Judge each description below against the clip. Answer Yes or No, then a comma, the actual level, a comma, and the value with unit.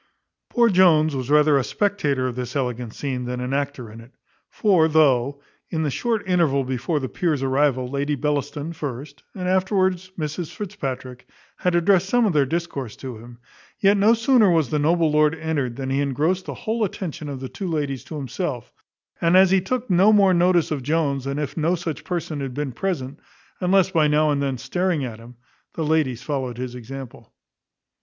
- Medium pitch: Yes, medium, 150 Hz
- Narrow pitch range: No, average, 5.1 semitones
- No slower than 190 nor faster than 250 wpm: Yes, average, 195 wpm